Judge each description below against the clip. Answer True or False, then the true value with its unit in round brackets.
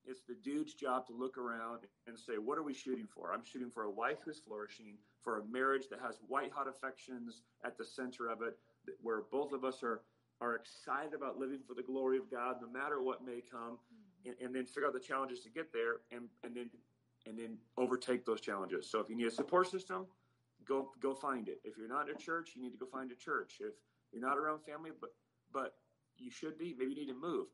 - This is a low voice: True (125 Hz)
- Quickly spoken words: True (240 wpm)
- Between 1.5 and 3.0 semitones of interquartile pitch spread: True (2.7 semitones)